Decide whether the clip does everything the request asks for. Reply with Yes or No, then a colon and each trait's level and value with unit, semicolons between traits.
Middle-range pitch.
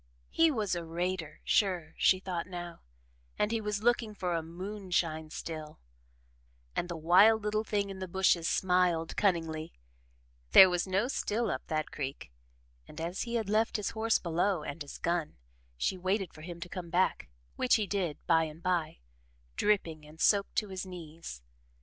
Yes: medium, 180 Hz